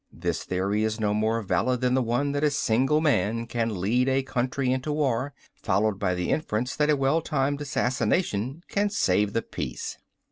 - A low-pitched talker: Yes, low, 125 Hz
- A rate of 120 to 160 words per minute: No, average, 185 wpm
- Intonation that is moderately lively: Yes, average, 4.6 semitones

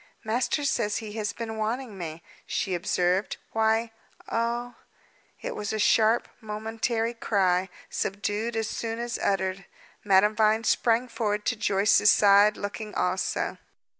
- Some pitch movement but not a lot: No, narrow, 2.2 semitones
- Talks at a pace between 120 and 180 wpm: Yes, slow, 135 wpm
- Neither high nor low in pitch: No, high, 215 Hz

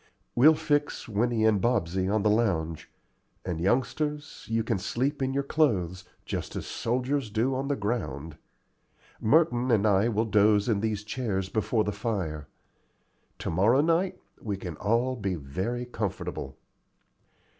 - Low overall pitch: Yes, low, 110 Hz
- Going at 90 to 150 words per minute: Yes, average, 145 wpm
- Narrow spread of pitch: No, average, 4.6 semitones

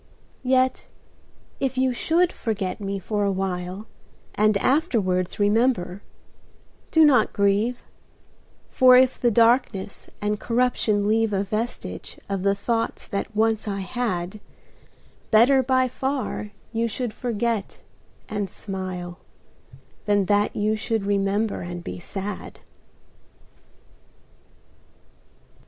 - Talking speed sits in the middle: No, slow, 110 wpm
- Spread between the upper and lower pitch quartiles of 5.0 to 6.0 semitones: No, average, 3.5 semitones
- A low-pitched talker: No, high, 215 Hz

